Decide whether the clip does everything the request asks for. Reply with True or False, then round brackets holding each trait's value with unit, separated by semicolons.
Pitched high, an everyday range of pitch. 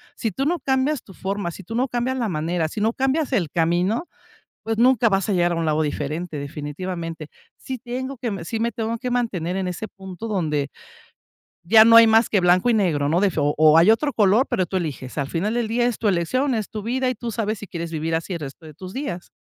False (195 Hz; 5.9 semitones)